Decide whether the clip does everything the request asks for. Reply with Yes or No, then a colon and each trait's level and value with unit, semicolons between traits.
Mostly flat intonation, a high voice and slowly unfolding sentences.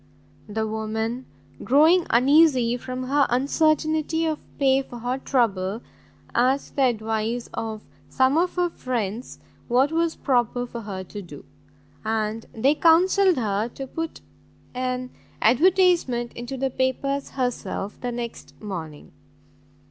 No: average, 4.2 semitones; very high, 250 Hz; slow, 125 wpm